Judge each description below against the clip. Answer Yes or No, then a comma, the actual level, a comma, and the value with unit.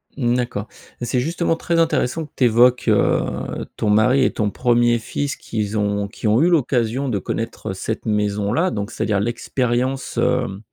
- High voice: No, low, 120 Hz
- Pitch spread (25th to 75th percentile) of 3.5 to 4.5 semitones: Yes, average, 4.0 semitones